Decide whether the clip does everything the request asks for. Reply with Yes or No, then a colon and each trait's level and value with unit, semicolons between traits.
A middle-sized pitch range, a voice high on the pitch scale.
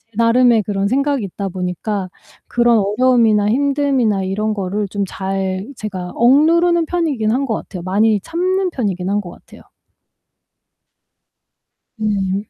Yes: average, 4.8 semitones; high, 215 Hz